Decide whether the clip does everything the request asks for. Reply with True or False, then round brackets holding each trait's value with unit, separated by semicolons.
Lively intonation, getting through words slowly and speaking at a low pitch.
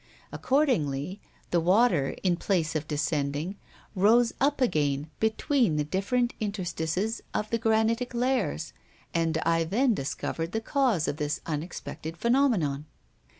False (6.8 semitones; 125 wpm; 185 Hz)